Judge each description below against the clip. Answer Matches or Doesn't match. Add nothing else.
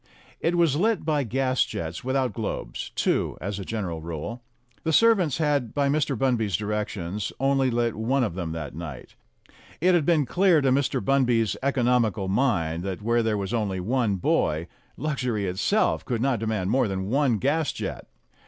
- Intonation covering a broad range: Matches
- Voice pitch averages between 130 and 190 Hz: Doesn't match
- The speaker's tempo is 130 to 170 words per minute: Doesn't match